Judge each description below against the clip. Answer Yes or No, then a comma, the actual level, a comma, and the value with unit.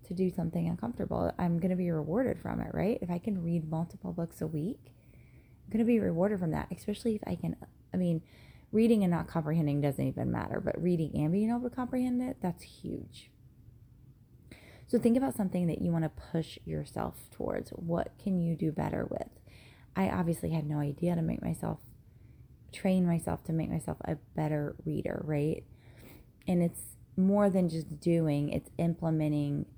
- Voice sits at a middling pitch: Yes, medium, 165 Hz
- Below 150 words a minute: No, average, 185 wpm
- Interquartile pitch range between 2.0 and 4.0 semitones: No, average, 4.4 semitones